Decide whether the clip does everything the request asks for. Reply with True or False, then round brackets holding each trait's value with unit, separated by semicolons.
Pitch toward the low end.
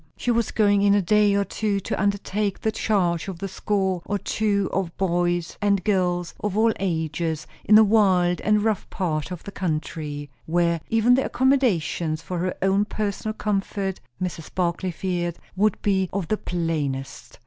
False (190 Hz)